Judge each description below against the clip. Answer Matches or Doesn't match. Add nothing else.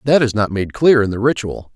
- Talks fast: Matches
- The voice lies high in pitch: Doesn't match